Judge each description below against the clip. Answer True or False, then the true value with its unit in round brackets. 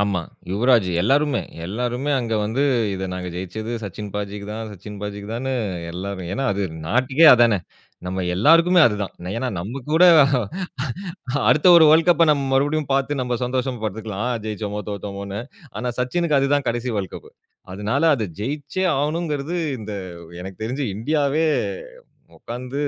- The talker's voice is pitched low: True (120 Hz)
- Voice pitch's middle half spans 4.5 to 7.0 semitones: True (5.6 semitones)